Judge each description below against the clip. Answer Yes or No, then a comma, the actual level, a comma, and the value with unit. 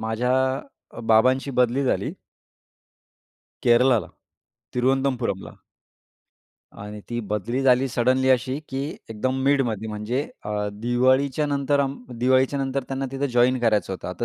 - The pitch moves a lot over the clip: No, average, 3.1 semitones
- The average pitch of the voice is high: No, low, 125 Hz